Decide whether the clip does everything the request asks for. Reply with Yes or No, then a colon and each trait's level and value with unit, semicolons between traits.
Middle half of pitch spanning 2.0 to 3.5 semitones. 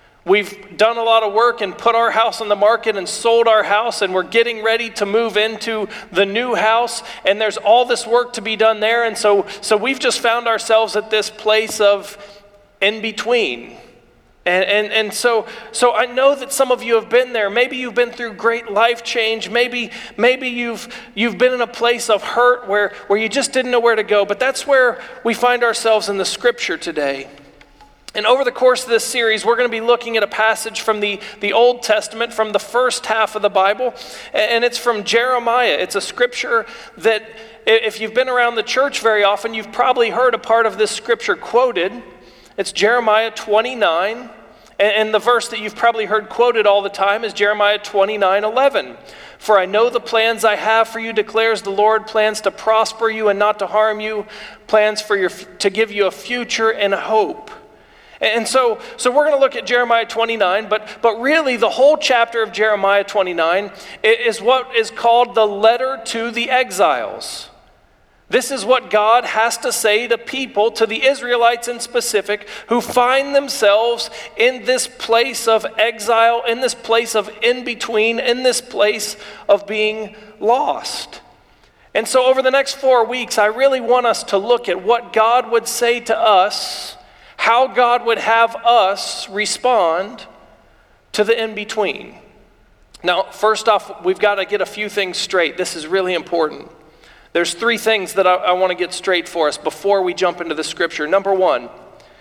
Yes: narrow, 2.5 semitones